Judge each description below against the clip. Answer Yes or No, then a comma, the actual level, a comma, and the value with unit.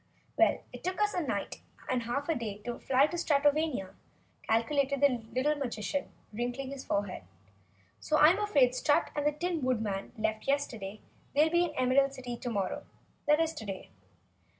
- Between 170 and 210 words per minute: Yes, average, 175 wpm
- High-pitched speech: Yes, very high, 275 Hz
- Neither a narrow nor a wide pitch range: Yes, average, 4.5 semitones